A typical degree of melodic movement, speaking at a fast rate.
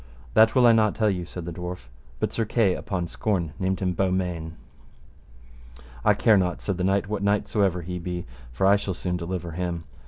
No: narrow, 2.3 semitones; fast, 210 wpm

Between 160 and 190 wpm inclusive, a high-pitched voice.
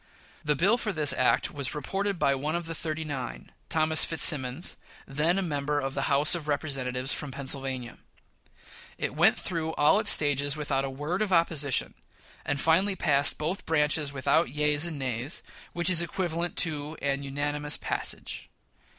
No: average, 165 wpm; medium, 150 Hz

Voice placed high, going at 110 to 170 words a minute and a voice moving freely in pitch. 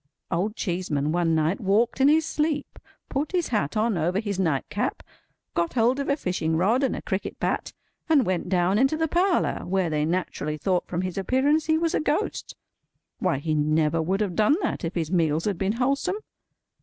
No: high, 195 Hz; average, 200 wpm; wide, 8.2 semitones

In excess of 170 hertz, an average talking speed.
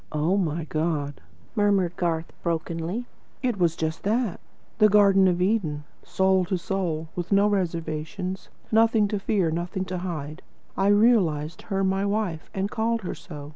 Yes: medium, 185 Hz; average, 155 wpm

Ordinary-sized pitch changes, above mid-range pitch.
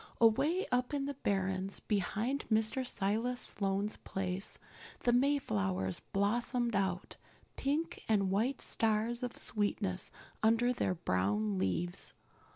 Yes: average, 4.7 semitones; high, 210 Hz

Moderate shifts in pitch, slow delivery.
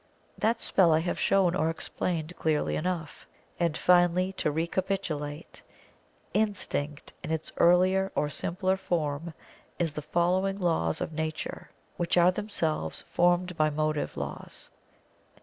Yes: average, 3.0 semitones; slow, 130 wpm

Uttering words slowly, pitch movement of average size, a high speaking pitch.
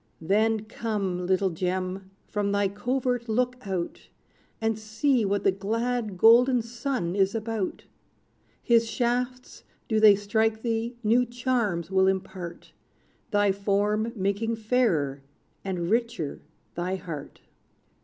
Yes: slow, 120 wpm; average, 3.5 semitones; high, 215 Hz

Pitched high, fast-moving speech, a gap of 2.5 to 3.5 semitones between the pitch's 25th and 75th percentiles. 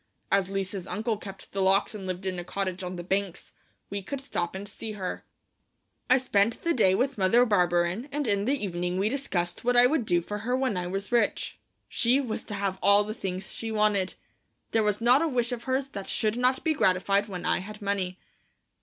No: high, 200 Hz; fast, 215 wpm; average, 4.2 semitones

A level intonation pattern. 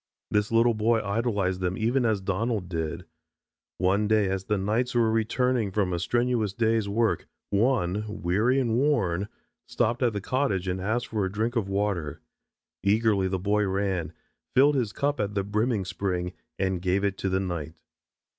No: average, 3.4 semitones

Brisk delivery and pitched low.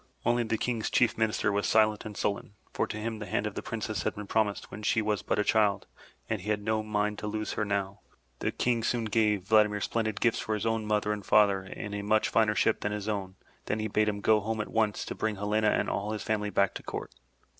Yes: fast, 250 wpm; low, 105 Hz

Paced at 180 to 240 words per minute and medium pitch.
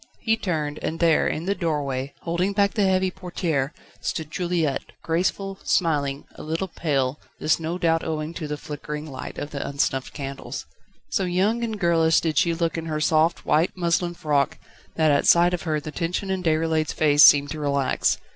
Yes: average, 185 wpm; medium, 160 Hz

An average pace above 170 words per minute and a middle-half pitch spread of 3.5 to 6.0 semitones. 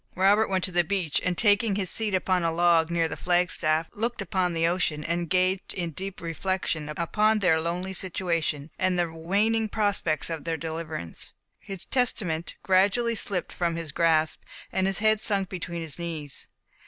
No: average, 180 wpm; average, 3.0 semitones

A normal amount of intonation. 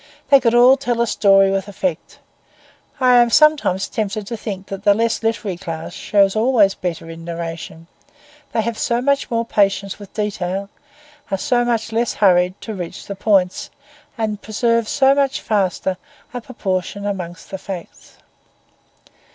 Yes: average, 3.7 semitones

